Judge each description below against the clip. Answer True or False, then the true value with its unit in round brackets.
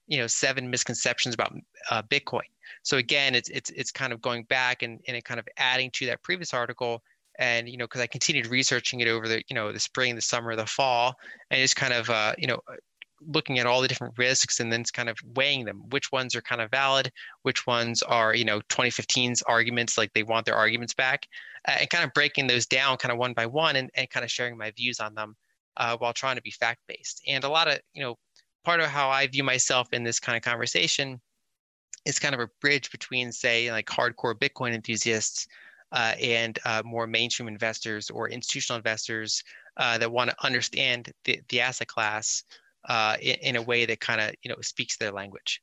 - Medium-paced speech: False (220 wpm)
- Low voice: True (120 Hz)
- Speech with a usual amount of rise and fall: False (2.2 semitones)